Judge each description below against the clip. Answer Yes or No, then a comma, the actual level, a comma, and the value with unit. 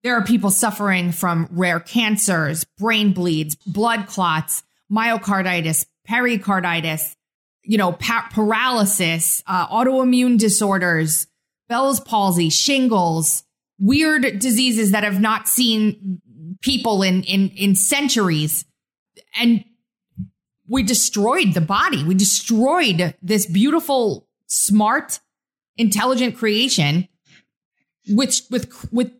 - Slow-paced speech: Yes, slow, 105 wpm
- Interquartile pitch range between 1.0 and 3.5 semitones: No, average, 4.9 semitones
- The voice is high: Yes, high, 205 Hz